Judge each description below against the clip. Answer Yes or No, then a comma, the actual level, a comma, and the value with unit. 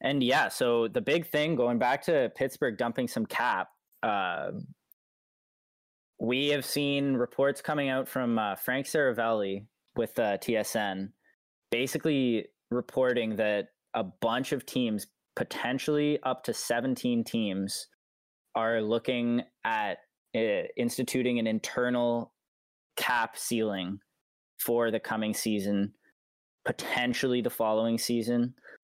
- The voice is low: Yes, low, 120 Hz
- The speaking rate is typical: No, slow, 115 wpm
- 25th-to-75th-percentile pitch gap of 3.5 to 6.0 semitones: No, average, 3.1 semitones